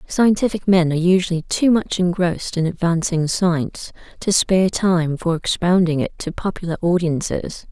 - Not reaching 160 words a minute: Yes, average, 150 wpm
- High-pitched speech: No, medium, 175 Hz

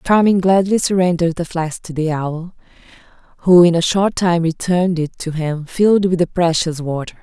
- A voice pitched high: No, medium, 170 Hz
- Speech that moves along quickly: No, average, 185 wpm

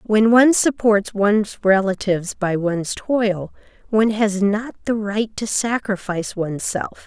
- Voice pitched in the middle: No, high, 210 Hz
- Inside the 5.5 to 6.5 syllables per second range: No, 4.5 syllables/s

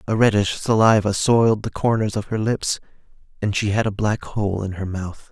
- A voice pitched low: Yes, low, 105 Hz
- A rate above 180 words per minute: Yes, fast, 205 wpm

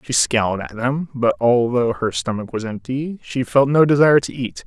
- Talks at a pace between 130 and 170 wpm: No, fast, 205 wpm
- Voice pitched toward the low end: Yes, low, 125 Hz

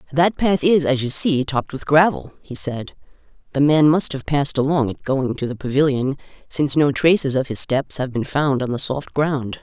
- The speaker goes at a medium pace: No, fast, 220 wpm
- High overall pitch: No, medium, 140 Hz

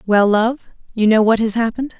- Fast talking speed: No, average, 180 wpm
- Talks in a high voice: Yes, high, 225 Hz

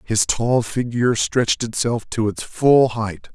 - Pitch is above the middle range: No, low, 115 Hz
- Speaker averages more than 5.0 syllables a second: No, 4.0 syllables/s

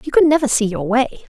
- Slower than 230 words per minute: No, fast, 265 wpm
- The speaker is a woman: Yes, female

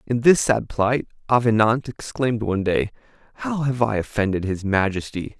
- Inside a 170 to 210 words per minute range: No, average, 155 wpm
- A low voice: Yes, low, 110 Hz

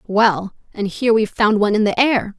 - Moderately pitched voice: No, high, 215 Hz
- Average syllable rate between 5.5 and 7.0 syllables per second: Yes, 5.6 syllables/s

